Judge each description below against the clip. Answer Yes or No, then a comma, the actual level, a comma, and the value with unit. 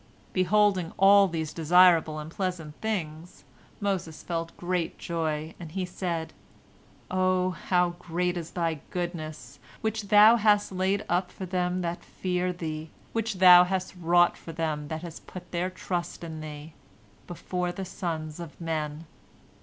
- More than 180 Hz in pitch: No, medium, 175 Hz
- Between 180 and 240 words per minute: No, average, 145 wpm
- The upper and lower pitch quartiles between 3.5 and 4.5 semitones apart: No, narrow, 2.4 semitones